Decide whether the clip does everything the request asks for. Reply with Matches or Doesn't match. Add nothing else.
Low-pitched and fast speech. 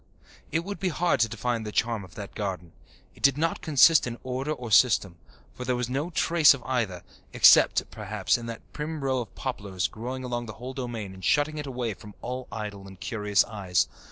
Matches